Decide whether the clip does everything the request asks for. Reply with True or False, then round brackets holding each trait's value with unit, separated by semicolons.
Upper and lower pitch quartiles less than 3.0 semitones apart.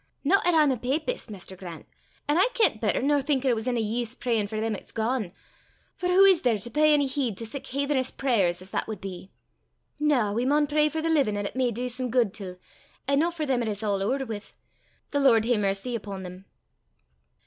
False (5.4 semitones)